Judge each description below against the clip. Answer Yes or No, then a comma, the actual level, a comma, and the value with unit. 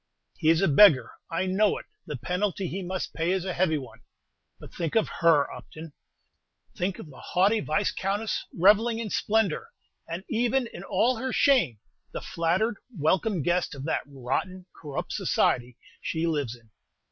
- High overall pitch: No, medium, 180 Hz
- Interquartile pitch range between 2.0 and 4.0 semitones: No, average, 4.8 semitones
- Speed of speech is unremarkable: Yes, average, 165 wpm